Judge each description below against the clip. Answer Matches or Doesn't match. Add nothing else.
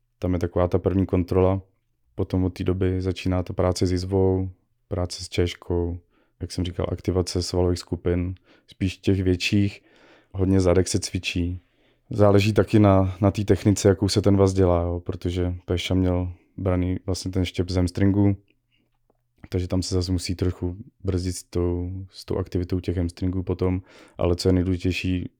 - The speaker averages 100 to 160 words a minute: Doesn't match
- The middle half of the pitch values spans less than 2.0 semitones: Matches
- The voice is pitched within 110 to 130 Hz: Doesn't match